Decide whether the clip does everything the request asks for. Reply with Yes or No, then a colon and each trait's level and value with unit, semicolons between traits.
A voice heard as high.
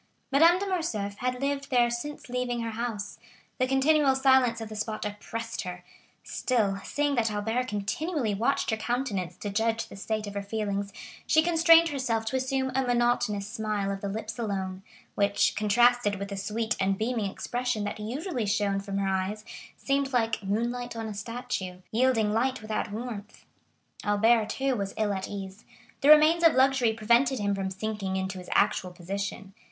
Yes: high, 220 Hz